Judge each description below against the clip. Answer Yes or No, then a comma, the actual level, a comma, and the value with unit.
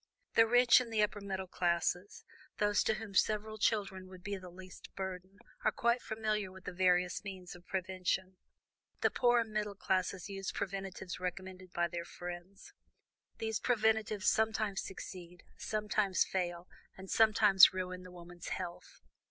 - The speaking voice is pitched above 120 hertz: Yes, high, 190 Hz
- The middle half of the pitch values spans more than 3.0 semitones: No, average, 2.7 semitones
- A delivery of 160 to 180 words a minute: No, average, 150 wpm